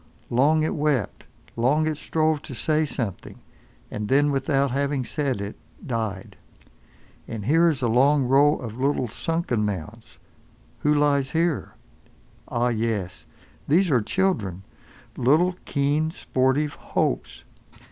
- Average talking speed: No, slow, 125 wpm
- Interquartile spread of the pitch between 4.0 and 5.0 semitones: Yes, average, 4.6 semitones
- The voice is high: No, medium, 140 Hz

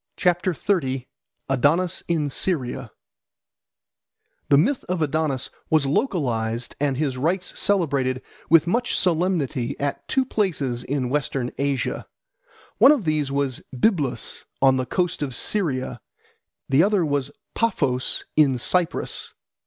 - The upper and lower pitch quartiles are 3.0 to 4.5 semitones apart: No, average, 5.2 semitones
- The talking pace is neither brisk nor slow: No, slow, 115 wpm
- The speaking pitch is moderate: Yes, medium, 145 Hz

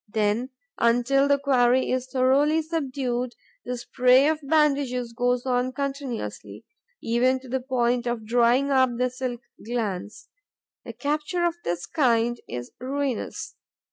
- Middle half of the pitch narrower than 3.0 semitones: Yes, narrow, 2.4 semitones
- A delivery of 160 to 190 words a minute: No, slow, 135 wpm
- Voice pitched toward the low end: No, very high, 255 Hz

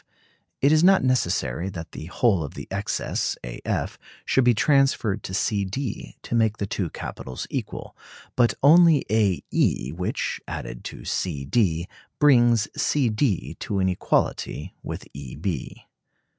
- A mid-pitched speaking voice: No, low, 105 Hz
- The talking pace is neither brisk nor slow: Yes, average, 155 wpm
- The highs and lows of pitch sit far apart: Yes, wide, 7.2 semitones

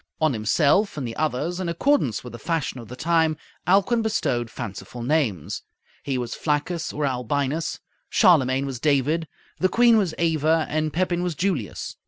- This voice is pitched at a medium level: Yes, medium, 155 Hz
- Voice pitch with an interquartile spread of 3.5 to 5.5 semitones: Yes, average, 5.0 semitones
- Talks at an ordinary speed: Yes, average, 165 wpm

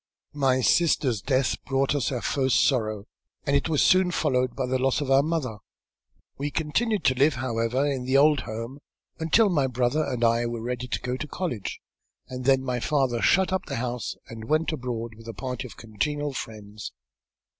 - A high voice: No, low, 130 Hz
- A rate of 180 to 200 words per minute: Yes, average, 190 wpm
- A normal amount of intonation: Yes, average, 3.5 semitones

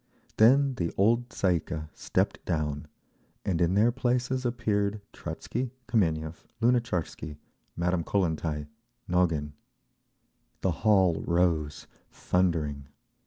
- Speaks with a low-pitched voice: Yes, very low, 90 Hz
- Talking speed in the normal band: No, slow, 105 wpm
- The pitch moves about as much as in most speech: No, wide, 6.1 semitones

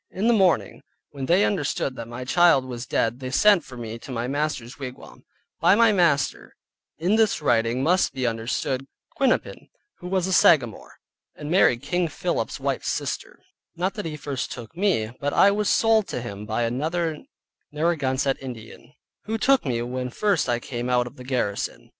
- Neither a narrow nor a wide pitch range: No, wide, 6.5 semitones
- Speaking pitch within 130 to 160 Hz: Yes, medium, 140 Hz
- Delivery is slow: No, average, 185 wpm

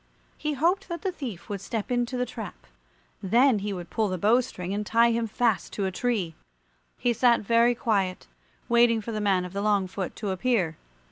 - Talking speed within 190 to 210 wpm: Yes, fast, 205 wpm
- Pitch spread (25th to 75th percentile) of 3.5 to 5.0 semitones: Yes, average, 3.8 semitones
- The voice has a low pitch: No, high, 220 Hz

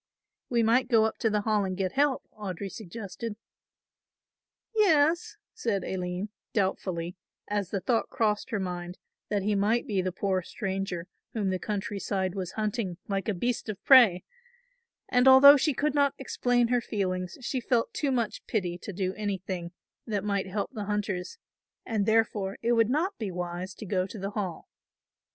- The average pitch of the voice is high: Yes, high, 205 Hz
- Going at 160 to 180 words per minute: Yes, average, 175 wpm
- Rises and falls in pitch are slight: No, average, 3.7 semitones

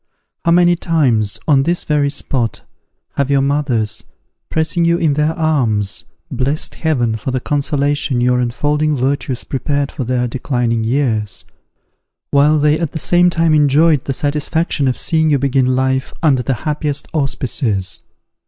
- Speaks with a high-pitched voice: No, medium, 140 Hz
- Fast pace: No, average, 150 wpm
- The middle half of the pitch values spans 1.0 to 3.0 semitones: No, average, 3.4 semitones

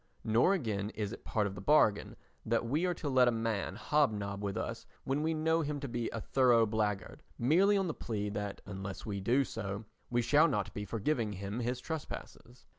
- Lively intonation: Yes, wide, 5.7 semitones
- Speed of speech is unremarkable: No, fast, 210 wpm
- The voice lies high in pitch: No, low, 115 Hz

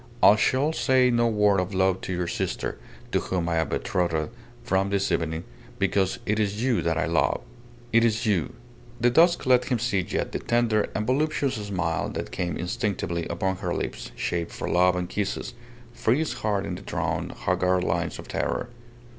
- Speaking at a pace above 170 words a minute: Yes, average, 185 wpm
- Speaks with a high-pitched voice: No, low, 100 Hz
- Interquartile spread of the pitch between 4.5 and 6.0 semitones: Yes, average, 4.9 semitones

